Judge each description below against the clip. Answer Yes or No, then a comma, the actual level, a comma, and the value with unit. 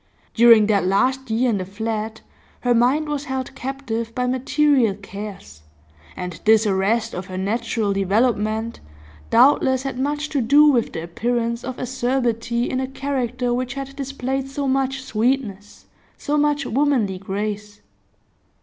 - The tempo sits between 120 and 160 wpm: Yes, average, 145 wpm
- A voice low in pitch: No, high, 240 Hz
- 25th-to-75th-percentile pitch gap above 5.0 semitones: No, average, 3.9 semitones